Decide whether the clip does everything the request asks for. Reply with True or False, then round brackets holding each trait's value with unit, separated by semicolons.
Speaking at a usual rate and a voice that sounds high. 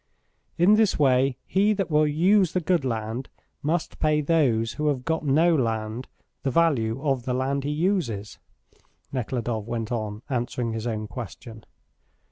False (155 wpm; 135 Hz)